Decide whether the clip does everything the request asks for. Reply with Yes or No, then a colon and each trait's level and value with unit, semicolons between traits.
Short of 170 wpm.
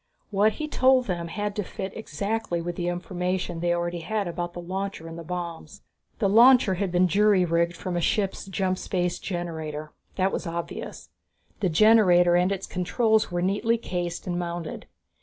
No: average, 175 wpm